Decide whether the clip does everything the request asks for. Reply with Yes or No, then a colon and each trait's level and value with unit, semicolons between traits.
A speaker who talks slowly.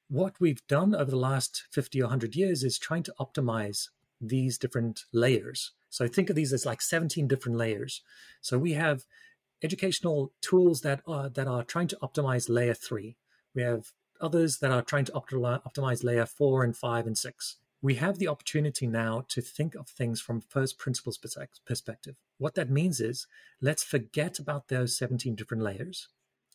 No: average, 175 wpm